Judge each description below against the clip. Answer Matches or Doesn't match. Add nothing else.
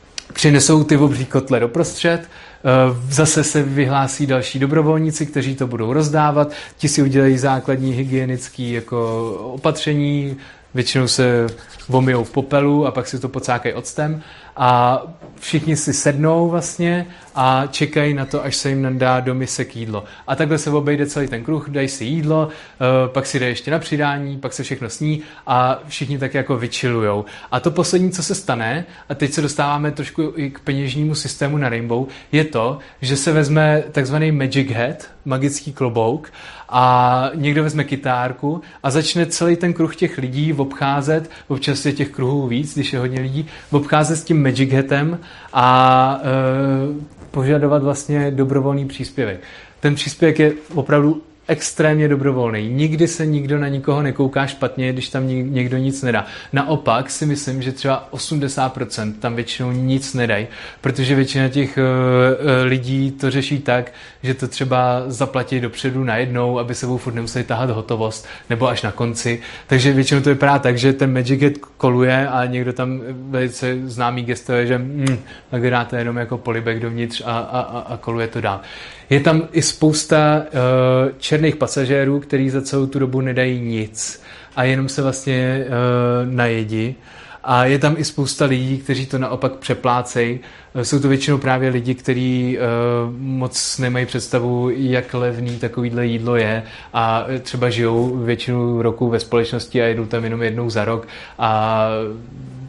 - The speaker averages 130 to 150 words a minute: Doesn't match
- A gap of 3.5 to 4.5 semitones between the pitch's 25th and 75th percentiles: Doesn't match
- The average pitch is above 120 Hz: Matches